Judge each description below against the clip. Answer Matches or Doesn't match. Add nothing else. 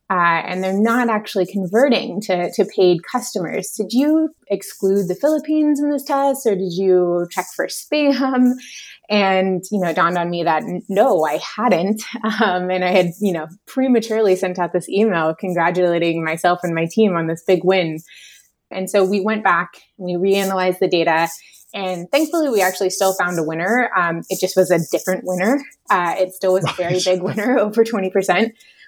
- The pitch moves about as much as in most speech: Matches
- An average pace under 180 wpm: Doesn't match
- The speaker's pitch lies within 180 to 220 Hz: Matches